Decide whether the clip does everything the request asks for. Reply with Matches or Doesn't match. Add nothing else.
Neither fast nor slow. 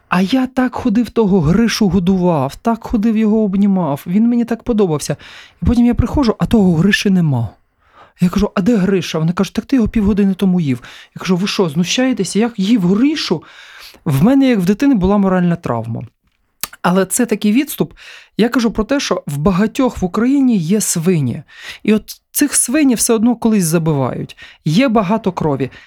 Doesn't match